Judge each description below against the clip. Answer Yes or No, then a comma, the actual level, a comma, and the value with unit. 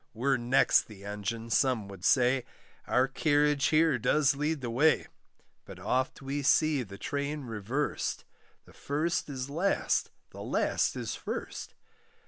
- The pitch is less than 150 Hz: Yes, low, 135 Hz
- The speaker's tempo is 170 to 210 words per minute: No, average, 140 wpm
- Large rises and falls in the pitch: No, average, 4.0 semitones